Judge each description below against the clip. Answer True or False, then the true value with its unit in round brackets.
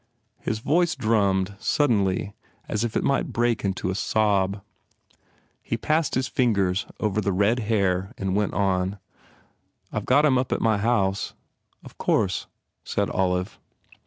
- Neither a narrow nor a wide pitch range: True (3.6 semitones)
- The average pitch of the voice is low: True (105 Hz)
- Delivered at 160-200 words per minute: False (150 wpm)